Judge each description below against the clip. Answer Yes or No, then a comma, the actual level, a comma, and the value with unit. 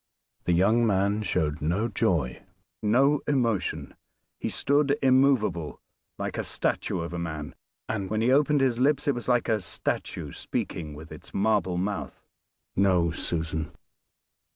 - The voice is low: Yes, low, 105 Hz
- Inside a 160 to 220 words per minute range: No, average, 145 wpm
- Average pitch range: No, wide, 6.8 semitones